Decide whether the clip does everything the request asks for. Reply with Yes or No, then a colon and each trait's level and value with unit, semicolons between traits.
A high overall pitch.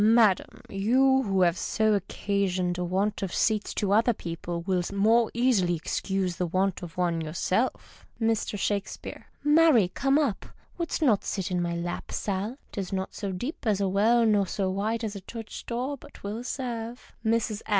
Yes: high, 200 Hz